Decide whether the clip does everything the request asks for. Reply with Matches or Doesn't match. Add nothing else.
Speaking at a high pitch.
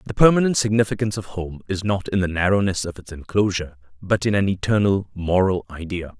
Doesn't match